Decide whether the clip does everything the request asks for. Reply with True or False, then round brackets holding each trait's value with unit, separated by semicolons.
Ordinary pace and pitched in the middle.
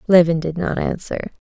True (165 wpm; 170 Hz)